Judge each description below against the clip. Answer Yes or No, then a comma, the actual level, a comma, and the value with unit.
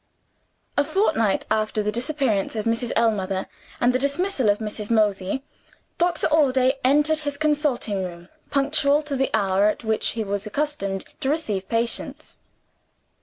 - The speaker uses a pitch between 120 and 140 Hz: No, high, 240 Hz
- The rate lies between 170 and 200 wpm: No, average, 145 wpm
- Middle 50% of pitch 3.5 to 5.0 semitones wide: No, wide, 5.6 semitones